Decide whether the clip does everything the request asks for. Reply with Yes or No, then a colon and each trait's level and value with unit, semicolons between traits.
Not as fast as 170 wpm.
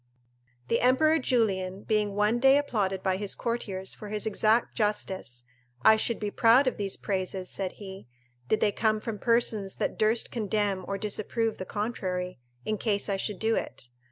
No: average, 175 wpm